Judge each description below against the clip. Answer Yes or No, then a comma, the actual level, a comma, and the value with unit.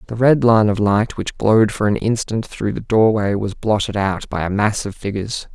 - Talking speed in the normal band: No, fast, 225 wpm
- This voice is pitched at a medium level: No, low, 105 Hz